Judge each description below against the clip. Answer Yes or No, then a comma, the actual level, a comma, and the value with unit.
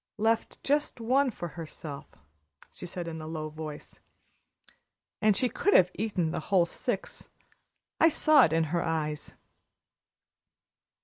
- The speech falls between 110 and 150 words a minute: Yes, slow, 135 wpm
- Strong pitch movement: Yes, wide, 6.3 semitones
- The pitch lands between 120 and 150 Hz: No, medium, 175 Hz